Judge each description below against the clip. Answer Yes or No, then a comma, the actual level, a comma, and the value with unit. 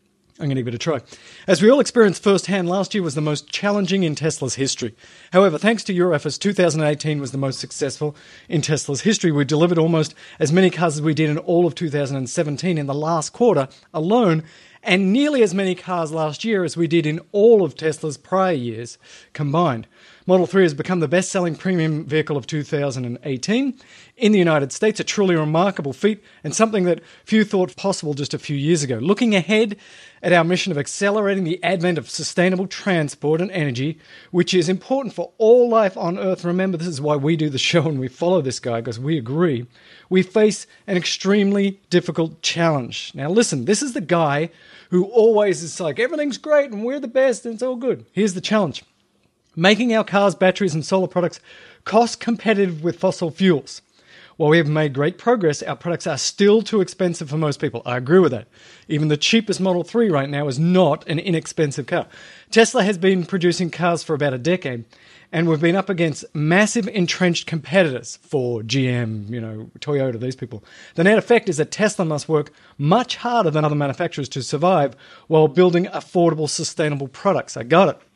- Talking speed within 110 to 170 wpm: No, average, 195 wpm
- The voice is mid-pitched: Yes, medium, 170 Hz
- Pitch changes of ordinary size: Yes, average, 4.4 semitones